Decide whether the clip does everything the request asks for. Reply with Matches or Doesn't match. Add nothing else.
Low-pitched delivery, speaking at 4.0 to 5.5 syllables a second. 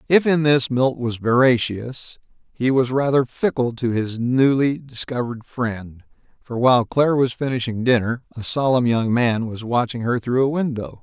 Matches